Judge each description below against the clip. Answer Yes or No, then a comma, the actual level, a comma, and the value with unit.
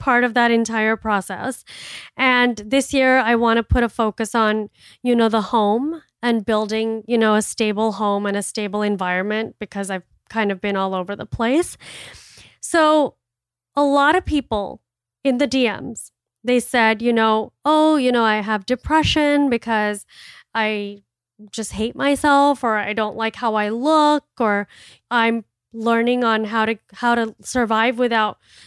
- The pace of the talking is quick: No, average, 165 wpm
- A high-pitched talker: Yes, high, 225 Hz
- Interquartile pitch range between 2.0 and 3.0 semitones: Yes, average, 2.7 semitones